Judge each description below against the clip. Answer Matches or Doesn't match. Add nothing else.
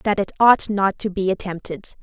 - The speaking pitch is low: Doesn't match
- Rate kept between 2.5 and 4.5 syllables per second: Doesn't match